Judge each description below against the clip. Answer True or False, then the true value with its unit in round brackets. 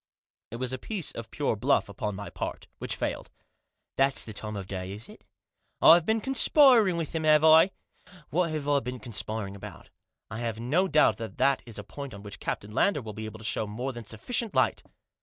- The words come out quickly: True (220 wpm)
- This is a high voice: False (125 Hz)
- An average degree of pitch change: False (6.6 semitones)